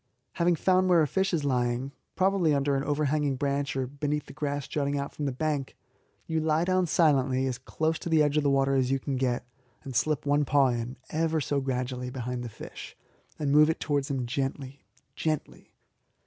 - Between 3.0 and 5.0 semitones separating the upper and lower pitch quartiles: No, narrow, 2.6 semitones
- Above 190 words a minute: Yes, fast, 205 wpm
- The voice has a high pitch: No, medium, 140 Hz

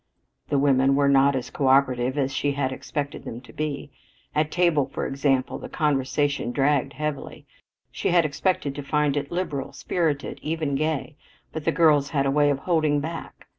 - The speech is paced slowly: No, average, 175 wpm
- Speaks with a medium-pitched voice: Yes, medium, 145 Hz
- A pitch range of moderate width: No, narrow, 1.9 semitones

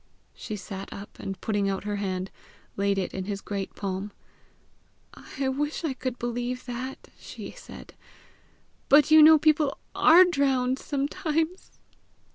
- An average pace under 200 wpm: Yes, average, 140 wpm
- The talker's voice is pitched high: Yes, very high, 250 Hz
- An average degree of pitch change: No, wide, 6.8 semitones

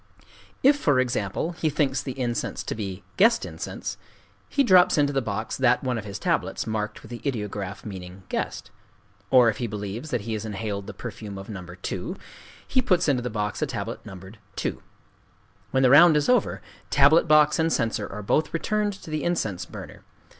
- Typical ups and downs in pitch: No, wide, 6.7 semitones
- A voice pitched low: Yes, low, 120 Hz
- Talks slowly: No, average, 190 wpm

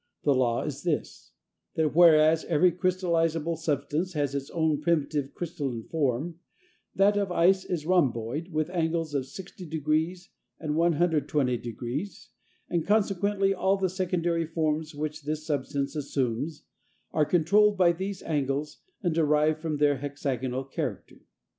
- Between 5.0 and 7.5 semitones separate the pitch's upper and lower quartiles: No, average, 3.3 semitones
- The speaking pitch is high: No, medium, 155 Hz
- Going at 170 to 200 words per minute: No, slow, 135 wpm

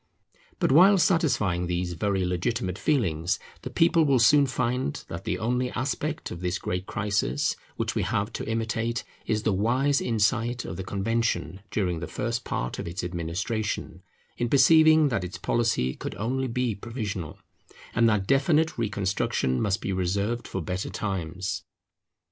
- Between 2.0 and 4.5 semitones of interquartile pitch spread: No, average, 5.3 semitones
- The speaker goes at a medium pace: Yes, average, 155 wpm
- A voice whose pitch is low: Yes, low, 110 Hz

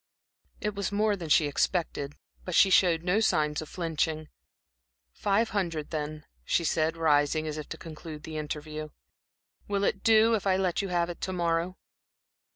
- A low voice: No, medium, 165 Hz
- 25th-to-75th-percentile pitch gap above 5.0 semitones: No, average, 3.9 semitones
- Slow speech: No, average, 170 wpm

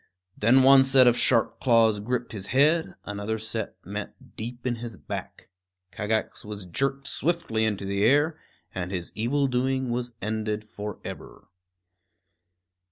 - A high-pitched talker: No, low, 115 Hz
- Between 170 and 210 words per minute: No, average, 140 wpm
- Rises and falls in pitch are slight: No, average, 3.9 semitones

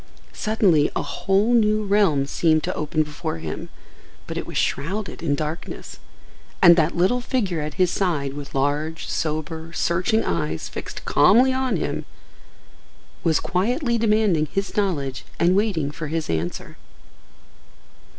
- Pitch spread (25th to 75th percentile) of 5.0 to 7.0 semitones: Yes, wide, 5.6 semitones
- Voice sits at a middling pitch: Yes, medium, 170 Hz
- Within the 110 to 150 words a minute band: Yes, average, 140 wpm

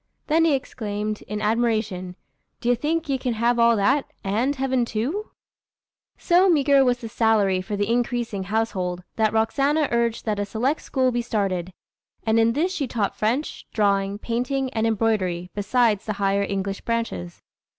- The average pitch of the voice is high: Yes, high, 225 Hz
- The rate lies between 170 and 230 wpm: No, average, 160 wpm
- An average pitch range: Yes, average, 4.0 semitones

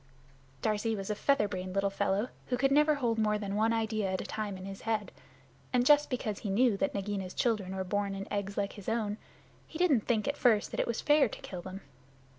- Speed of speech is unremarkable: No, fast, 235 wpm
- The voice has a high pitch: Yes, high, 210 Hz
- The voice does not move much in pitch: No, average, 3.4 semitones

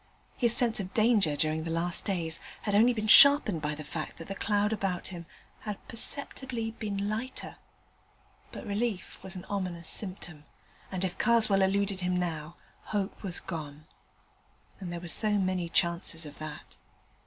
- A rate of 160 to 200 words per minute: Yes, average, 165 wpm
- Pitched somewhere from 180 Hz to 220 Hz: Yes, high, 190 Hz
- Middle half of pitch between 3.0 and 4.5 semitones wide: Yes, average, 4.1 semitones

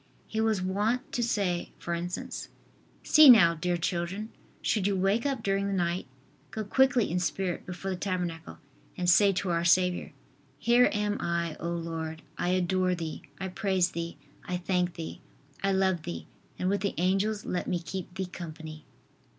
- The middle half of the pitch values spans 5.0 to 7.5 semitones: No, average, 2.7 semitones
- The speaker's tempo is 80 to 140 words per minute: No, average, 175 wpm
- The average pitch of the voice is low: No, medium, 185 Hz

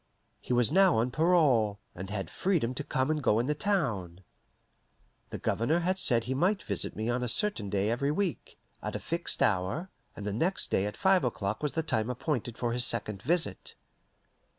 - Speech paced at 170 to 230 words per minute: Yes, average, 195 wpm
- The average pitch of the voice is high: No, low, 125 Hz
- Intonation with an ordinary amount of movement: No, wide, 7.4 semitones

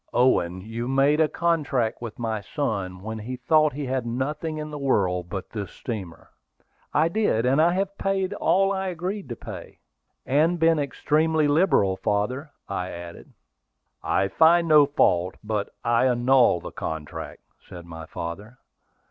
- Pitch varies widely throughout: Yes, wide, 7.5 semitones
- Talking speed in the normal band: Yes, average, 155 wpm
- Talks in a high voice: No, low, 130 Hz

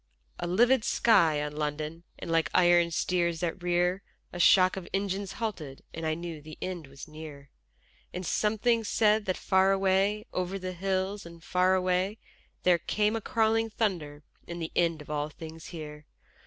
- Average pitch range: Yes, average, 3.4 semitones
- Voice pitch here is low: No, medium, 180 Hz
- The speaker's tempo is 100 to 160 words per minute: No, average, 175 wpm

